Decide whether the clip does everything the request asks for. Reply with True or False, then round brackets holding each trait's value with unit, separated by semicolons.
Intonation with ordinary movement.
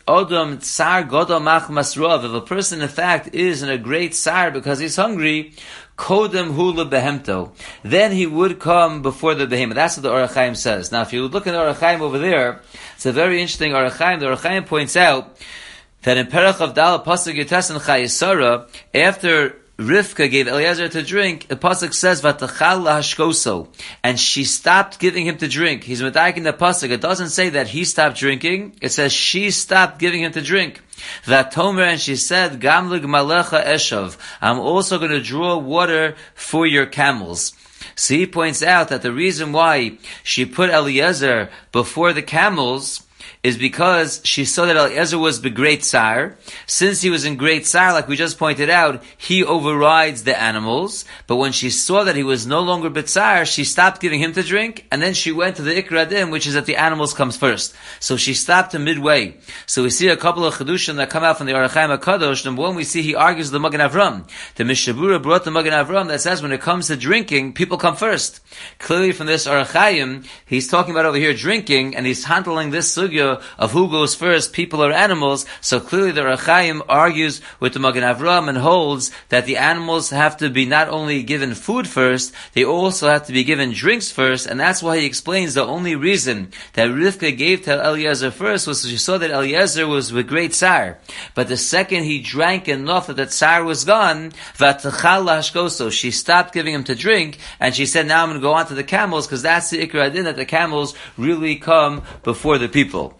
True (4.1 semitones)